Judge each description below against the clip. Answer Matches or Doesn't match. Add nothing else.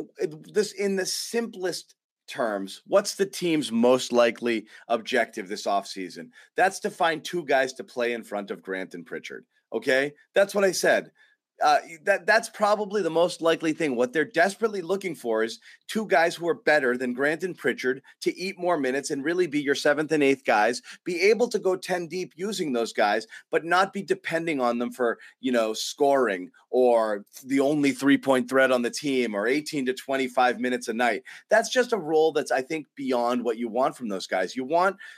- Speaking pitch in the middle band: Matches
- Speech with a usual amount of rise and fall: Doesn't match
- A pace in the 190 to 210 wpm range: Matches